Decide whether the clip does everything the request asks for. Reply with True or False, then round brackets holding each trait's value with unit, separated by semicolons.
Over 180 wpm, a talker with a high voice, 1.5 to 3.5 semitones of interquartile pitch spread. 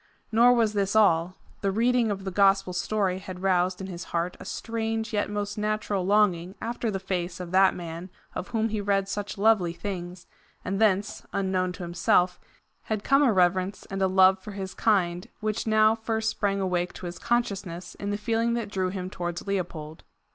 True (190 wpm; 195 Hz; 2.8 semitones)